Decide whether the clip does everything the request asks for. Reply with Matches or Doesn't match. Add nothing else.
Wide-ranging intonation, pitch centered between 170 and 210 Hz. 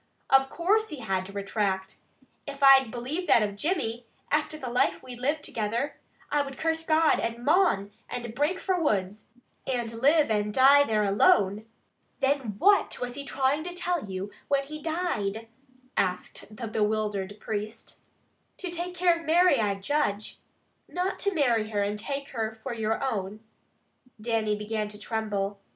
Doesn't match